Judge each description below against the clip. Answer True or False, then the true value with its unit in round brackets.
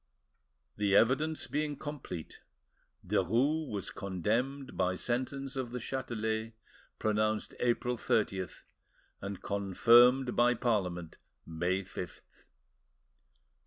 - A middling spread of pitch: True (4.9 semitones)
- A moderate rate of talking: False (90 wpm)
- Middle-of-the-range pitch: False (115 Hz)